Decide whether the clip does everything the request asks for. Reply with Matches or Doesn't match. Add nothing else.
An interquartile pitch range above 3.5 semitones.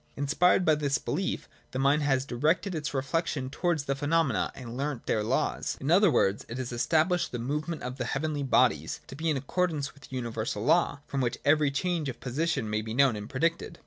Matches